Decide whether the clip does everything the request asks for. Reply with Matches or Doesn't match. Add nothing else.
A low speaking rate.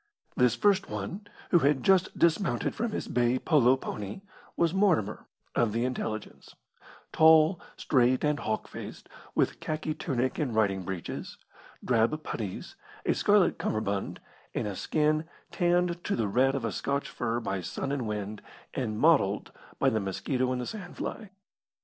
Doesn't match